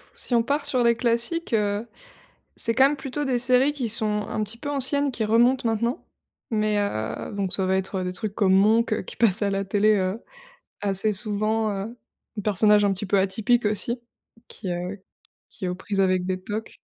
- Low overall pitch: No, high, 215 Hz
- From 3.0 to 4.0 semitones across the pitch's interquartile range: Yes, average, 3.3 semitones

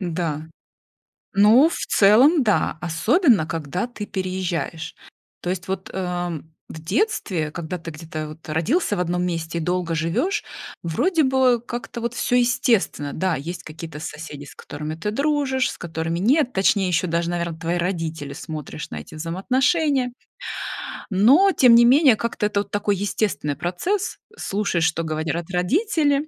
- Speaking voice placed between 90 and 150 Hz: No, medium, 185 Hz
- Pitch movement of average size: No, wide, 6.9 semitones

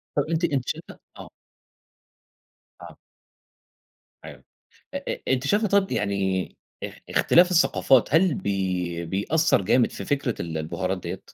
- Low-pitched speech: Yes, low, 120 Hz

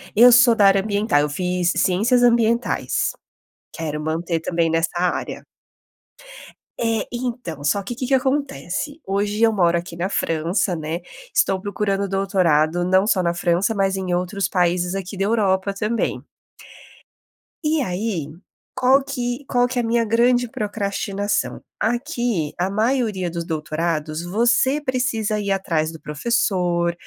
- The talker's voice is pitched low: No, high, 195 Hz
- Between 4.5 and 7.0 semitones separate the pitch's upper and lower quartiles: Yes, average, 5.2 semitones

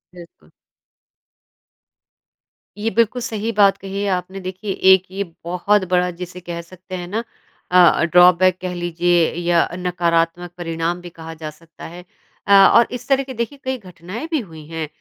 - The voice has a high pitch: No, medium, 180 Hz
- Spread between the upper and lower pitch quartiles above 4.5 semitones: No, average, 2.8 semitones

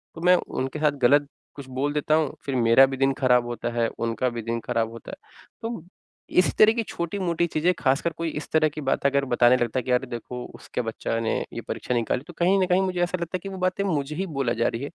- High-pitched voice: No, medium, 140 Hz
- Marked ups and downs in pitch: Yes, wide, 6.0 semitones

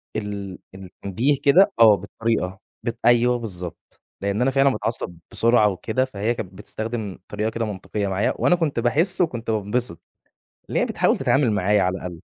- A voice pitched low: Yes, low, 110 Hz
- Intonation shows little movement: No, average, 3.7 semitones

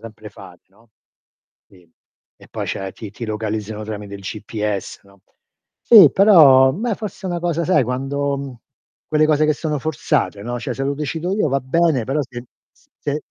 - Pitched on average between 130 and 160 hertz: Yes, low, 135 Hz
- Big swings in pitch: Yes, wide, 6.3 semitones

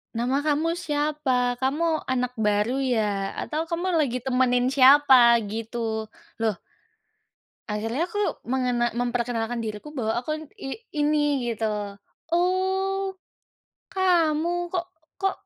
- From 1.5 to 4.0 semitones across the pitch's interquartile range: No, average, 4.7 semitones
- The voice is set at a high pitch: Yes, very high, 260 Hz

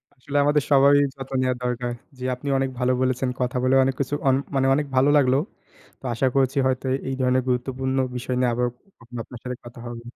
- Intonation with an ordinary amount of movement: No, narrow, 1.3 semitones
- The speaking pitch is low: Yes, low, 130 Hz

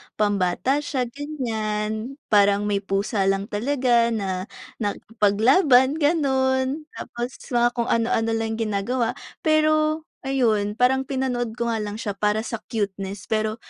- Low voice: No, high, 230 Hz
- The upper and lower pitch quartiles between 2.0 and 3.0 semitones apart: No, average, 4.1 semitones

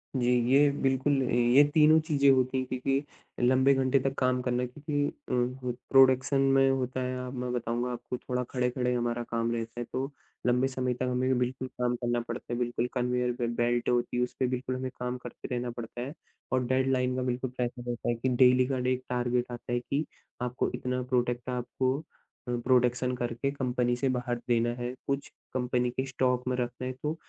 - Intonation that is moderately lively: No, narrow, 1.1 semitones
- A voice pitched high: No, low, 125 Hz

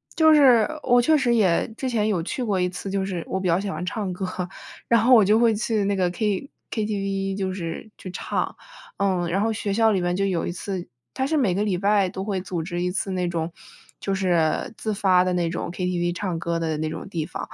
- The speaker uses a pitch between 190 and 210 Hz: Yes, high, 195 Hz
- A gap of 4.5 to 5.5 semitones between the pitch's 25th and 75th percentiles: No, average, 3.2 semitones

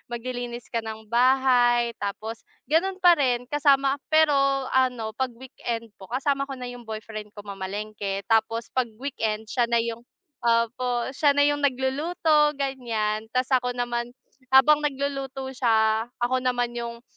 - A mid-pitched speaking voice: No, high, 245 Hz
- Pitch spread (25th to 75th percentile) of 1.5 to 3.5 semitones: Yes, average, 3.1 semitones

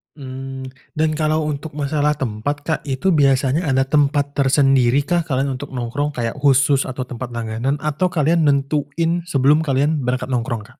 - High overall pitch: No, medium, 140 Hz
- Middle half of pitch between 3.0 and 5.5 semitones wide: No, narrow, 2.5 semitones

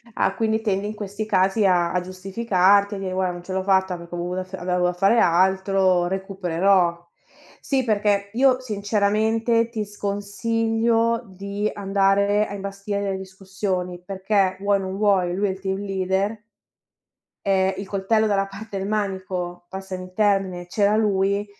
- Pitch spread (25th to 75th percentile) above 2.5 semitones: No, narrow, 1.6 semitones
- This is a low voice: No, high, 195 Hz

